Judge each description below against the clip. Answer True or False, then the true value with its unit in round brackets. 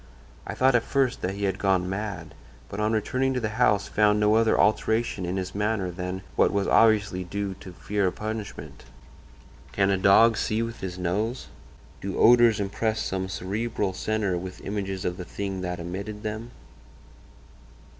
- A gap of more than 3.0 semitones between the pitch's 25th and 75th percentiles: False (2.7 semitones)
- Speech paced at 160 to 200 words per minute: True (175 wpm)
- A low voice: True (100 Hz)